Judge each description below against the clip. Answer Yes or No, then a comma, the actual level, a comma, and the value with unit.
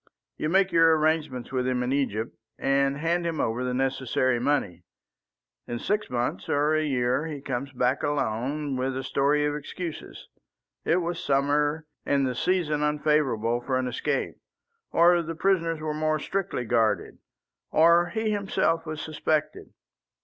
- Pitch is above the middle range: No, medium, 145 Hz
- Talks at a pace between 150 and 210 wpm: Yes, average, 155 wpm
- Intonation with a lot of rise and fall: No, average, 4.0 semitones